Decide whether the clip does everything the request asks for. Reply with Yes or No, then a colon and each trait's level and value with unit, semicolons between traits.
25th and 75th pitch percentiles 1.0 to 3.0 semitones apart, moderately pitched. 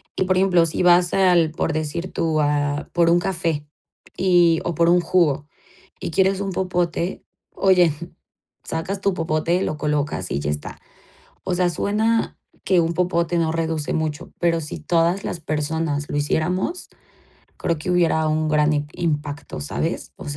Yes: average, 2.7 semitones; medium, 165 Hz